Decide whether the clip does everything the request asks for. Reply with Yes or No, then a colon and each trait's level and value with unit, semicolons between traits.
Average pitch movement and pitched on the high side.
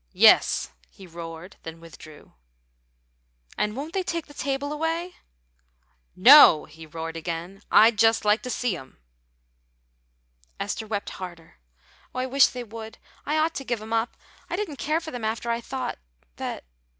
No: wide, 8.1 semitones; high, 225 Hz